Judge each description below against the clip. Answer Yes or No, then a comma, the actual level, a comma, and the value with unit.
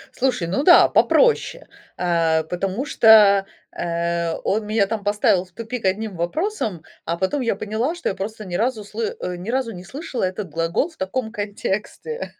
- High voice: Yes, high, 205 Hz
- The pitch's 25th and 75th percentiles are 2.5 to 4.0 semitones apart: No, average, 5.1 semitones